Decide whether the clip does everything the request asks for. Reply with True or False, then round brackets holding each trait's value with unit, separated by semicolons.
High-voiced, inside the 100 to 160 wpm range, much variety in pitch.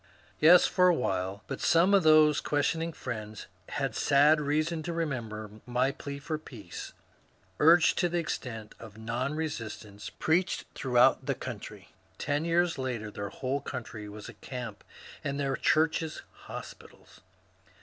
False (140 Hz; 145 wpm; 6.0 semitones)